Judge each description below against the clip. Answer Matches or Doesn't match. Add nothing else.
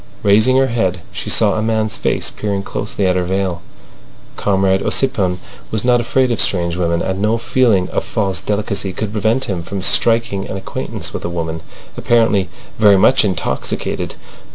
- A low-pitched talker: Matches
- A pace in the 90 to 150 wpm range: Doesn't match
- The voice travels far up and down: Doesn't match